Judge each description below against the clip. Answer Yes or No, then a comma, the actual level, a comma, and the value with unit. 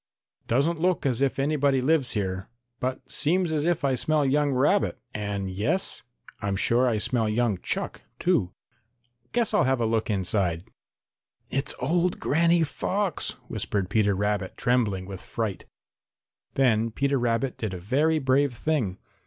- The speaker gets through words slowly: No, average, 150 wpm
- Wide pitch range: Yes, wide, 6.1 semitones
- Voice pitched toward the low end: Yes, low, 125 Hz